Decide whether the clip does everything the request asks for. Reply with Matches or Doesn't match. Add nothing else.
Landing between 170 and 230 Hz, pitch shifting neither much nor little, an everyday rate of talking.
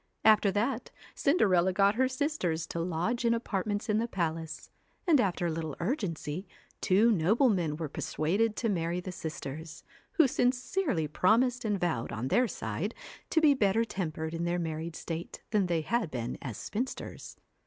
Doesn't match